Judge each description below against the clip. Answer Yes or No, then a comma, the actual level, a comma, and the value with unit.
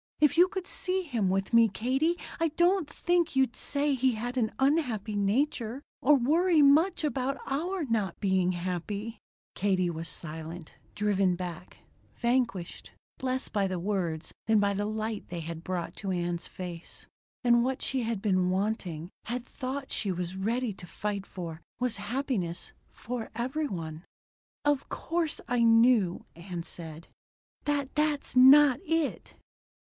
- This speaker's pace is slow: No, average, 150 wpm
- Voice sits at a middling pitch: No, high, 225 Hz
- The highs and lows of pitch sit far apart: Yes, wide, 6.7 semitones